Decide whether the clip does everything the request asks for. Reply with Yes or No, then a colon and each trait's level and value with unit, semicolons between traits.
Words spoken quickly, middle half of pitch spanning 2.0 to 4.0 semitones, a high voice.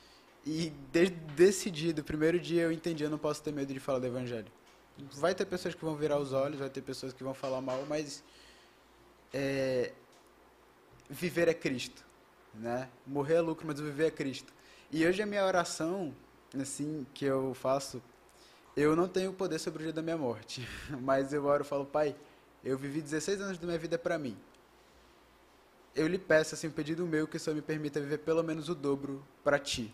No: fast, 195 wpm; average, 3.5 semitones; medium, 150 Hz